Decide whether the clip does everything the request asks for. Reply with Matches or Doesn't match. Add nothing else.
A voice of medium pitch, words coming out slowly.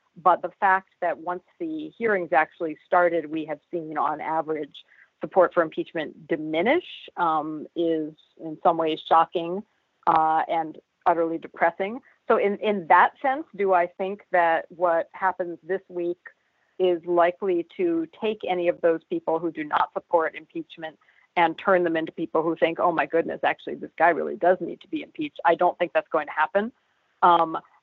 Doesn't match